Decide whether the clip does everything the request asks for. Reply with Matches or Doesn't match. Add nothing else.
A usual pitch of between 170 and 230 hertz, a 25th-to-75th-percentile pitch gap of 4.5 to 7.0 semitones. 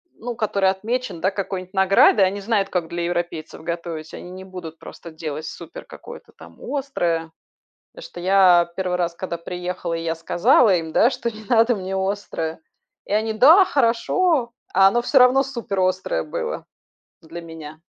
Matches